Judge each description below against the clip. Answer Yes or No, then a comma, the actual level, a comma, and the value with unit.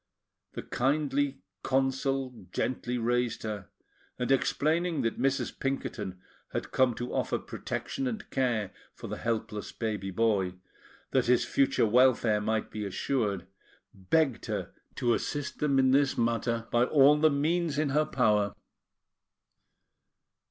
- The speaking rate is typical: No, slow, 130 wpm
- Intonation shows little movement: No, average, 3.8 semitones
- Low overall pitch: Yes, low, 125 Hz